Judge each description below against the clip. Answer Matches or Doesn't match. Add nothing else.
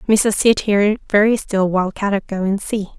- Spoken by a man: Doesn't match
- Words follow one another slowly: Doesn't match